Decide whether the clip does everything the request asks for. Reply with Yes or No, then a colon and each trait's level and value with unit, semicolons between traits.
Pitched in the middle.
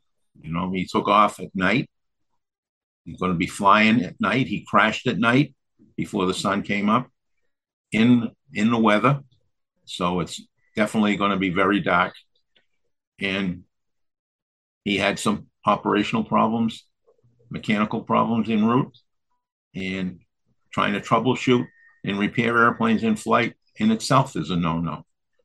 No: low, 115 Hz